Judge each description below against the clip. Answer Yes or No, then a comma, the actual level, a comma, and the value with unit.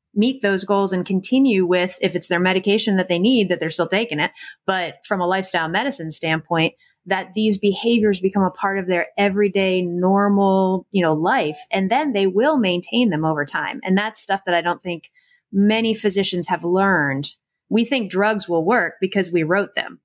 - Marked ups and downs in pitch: No, average, 2.7 semitones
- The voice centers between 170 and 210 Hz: Yes, high, 190 Hz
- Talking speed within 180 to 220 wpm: Yes, average, 195 wpm